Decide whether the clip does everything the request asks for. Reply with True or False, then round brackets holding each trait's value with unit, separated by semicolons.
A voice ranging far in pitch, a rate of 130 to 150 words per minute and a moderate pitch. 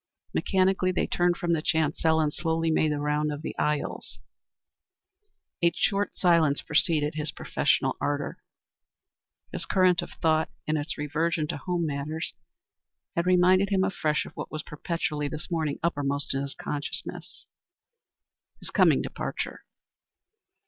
False (2.7 semitones; 140 wpm; 160 Hz)